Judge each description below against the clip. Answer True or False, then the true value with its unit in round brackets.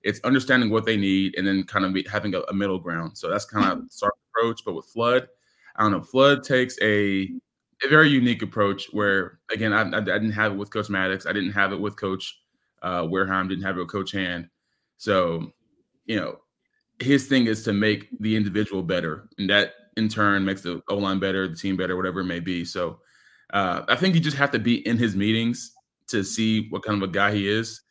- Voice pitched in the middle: False (100 Hz)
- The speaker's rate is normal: False (230 wpm)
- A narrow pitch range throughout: False (3.0 semitones)